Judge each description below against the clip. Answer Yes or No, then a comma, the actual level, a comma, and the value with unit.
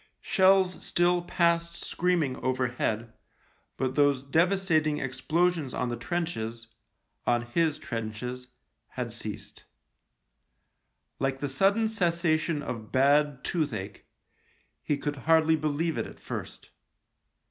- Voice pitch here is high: No, medium, 150 Hz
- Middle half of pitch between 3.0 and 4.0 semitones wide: No, average, 5.1 semitones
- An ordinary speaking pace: No, slow, 115 wpm